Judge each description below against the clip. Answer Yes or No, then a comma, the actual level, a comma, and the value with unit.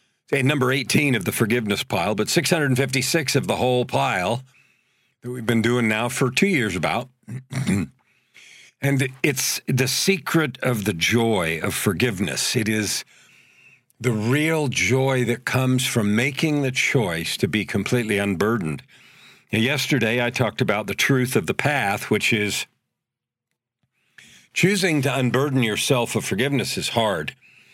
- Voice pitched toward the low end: Yes, low, 125 Hz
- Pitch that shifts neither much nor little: Yes, average, 3.2 semitones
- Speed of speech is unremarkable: Yes, average, 145 wpm